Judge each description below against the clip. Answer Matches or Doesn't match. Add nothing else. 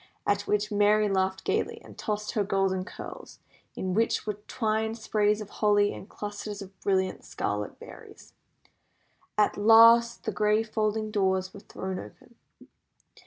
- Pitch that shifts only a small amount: Matches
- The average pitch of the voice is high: Matches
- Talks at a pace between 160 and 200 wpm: Doesn't match